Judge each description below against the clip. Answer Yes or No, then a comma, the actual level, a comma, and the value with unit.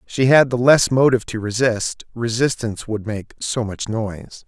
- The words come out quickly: No, average, 175 wpm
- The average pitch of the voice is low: Yes, low, 115 Hz